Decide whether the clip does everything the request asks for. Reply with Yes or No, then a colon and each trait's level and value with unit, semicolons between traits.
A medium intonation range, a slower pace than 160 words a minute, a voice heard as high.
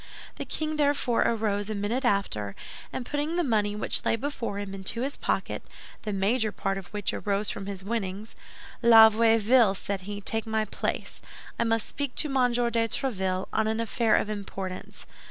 No: average, 3.0 semitones; average, 180 wpm; high, 220 Hz